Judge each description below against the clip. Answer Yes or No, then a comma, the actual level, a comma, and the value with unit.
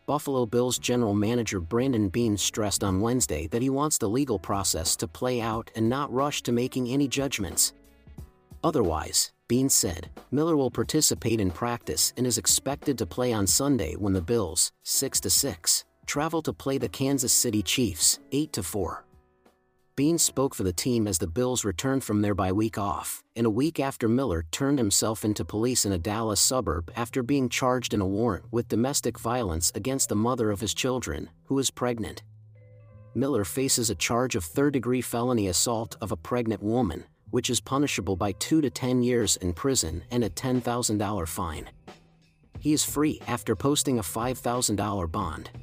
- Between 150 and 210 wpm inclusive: Yes, average, 175 wpm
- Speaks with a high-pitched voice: No, low, 115 Hz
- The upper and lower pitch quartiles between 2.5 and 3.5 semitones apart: No, average, 4.3 semitones